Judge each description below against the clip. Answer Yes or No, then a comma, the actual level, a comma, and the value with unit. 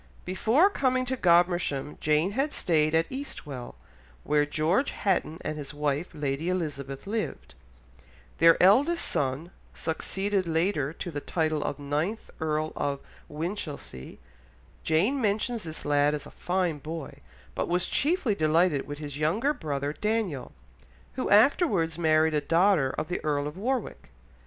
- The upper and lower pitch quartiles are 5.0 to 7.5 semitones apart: Yes, average, 5.3 semitones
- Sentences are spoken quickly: No, average, 140 wpm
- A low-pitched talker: No, medium, 165 Hz